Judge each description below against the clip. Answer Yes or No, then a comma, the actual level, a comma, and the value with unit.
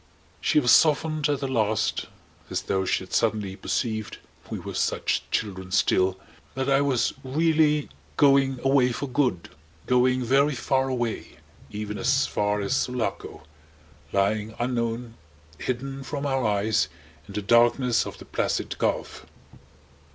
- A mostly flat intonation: No, average, 4.2 semitones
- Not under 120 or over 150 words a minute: Yes, average, 140 wpm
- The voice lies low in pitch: Yes, low, 125 Hz